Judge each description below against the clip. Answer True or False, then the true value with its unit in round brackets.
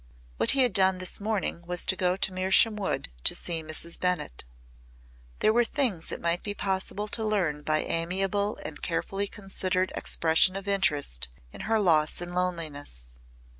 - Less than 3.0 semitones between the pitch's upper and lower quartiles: False (3.3 semitones)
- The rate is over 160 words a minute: True (170 wpm)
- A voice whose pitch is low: False (185 Hz)